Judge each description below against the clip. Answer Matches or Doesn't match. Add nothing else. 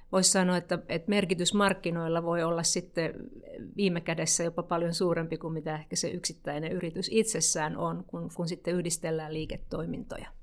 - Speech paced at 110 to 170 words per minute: Matches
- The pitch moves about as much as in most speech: Doesn't match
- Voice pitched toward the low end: Doesn't match